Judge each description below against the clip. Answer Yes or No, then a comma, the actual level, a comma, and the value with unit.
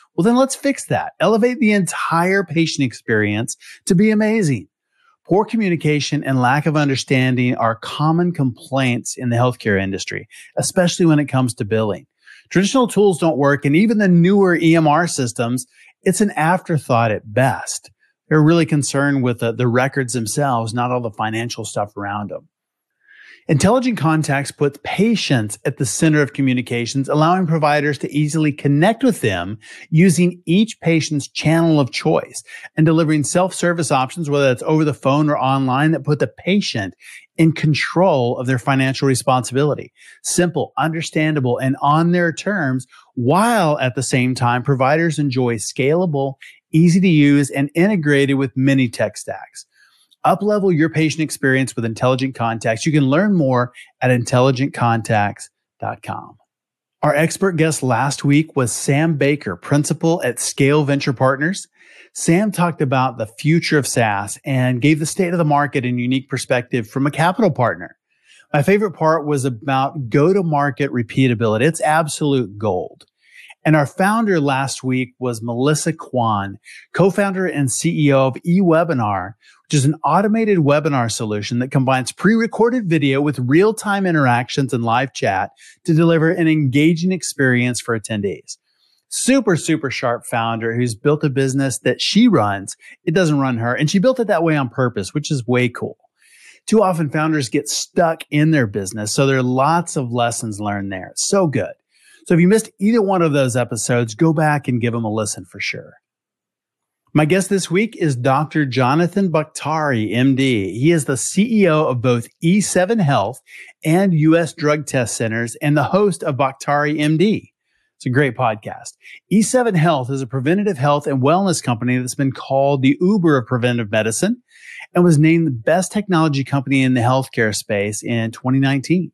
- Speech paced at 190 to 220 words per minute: No, average, 160 wpm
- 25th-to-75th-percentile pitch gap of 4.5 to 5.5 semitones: Yes, average, 4.9 semitones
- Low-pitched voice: No, medium, 145 Hz